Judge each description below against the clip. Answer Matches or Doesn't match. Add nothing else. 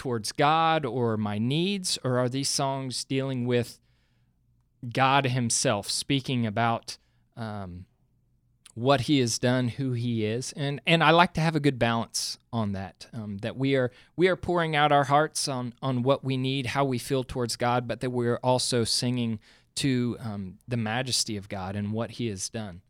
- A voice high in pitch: Doesn't match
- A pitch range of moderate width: Matches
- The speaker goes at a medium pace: Matches